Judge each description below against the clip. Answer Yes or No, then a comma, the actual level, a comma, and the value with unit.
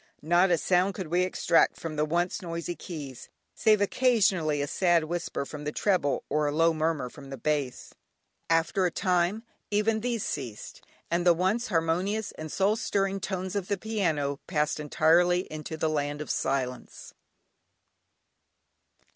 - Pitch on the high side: No, medium, 170 Hz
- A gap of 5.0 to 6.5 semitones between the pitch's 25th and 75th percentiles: No, average, 4.0 semitones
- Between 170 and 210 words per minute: No, average, 155 wpm